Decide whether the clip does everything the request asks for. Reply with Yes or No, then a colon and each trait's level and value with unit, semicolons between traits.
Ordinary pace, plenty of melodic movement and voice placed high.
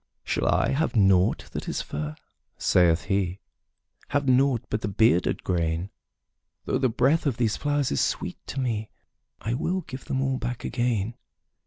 No: average, 165 wpm; wide, 5.7 semitones; low, 115 Hz